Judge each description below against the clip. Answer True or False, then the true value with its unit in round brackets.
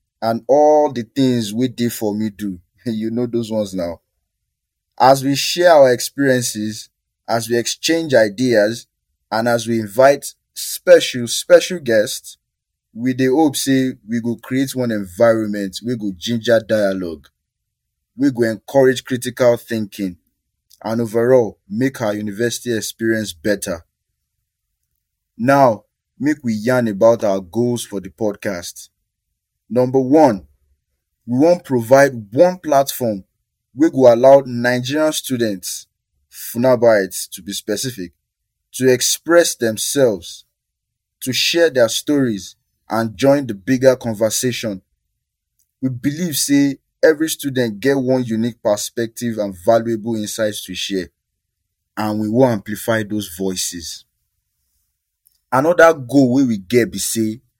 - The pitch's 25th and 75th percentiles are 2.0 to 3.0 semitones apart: False (3.9 semitones)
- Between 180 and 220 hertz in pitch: False (115 Hz)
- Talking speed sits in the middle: False (125 wpm)